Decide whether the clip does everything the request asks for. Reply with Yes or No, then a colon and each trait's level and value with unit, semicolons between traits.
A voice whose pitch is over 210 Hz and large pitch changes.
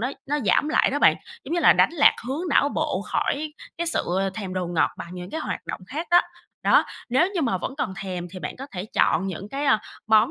Yes: high, 240 Hz; wide, 8.1 semitones